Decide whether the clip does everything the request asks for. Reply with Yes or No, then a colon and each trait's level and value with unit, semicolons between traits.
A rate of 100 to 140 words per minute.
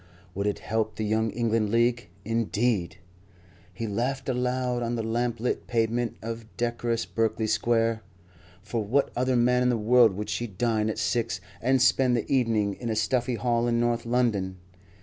No: average, 170 wpm